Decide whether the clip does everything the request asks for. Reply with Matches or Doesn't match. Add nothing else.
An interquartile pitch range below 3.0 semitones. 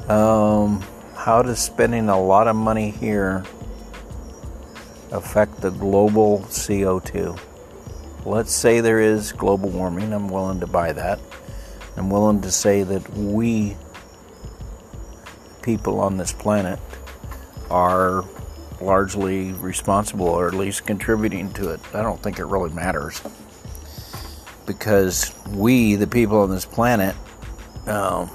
Matches